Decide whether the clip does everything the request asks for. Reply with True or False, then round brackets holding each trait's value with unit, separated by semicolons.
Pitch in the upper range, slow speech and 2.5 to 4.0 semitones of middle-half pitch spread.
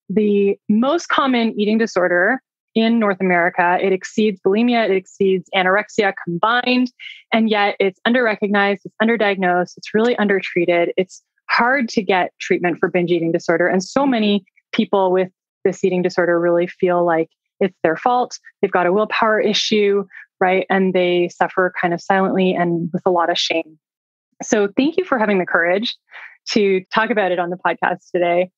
False (195 Hz; 170 wpm; 3.5 semitones)